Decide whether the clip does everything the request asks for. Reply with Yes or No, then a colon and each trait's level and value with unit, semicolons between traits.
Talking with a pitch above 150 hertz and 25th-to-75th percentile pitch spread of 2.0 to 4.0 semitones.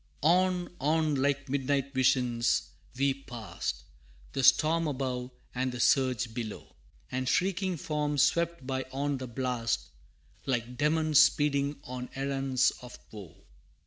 No: low, 135 Hz; average, 3.0 semitones